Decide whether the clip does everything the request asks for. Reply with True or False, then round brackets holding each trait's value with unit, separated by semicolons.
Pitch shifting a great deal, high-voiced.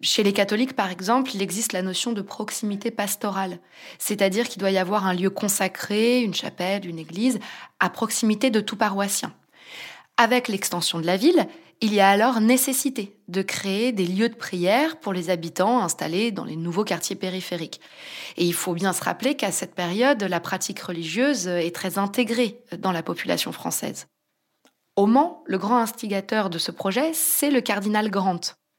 False (4.1 semitones; 205 Hz)